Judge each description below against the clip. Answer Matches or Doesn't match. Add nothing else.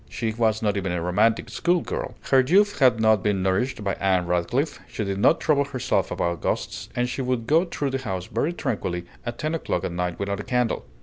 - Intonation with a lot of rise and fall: Matches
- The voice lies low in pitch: Matches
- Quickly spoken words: Matches